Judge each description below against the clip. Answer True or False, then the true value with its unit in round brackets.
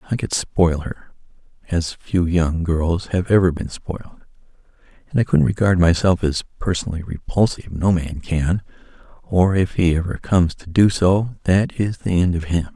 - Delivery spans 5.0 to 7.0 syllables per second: False (4.8 syllables/s)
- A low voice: True (90 Hz)